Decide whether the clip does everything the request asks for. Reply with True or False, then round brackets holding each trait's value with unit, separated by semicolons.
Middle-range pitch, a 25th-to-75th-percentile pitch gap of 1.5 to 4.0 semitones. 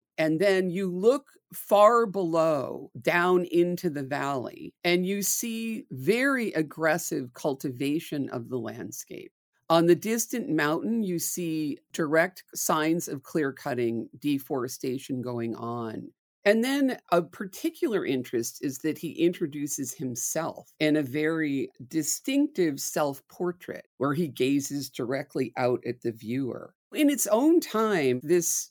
False (160 Hz; 5.6 semitones)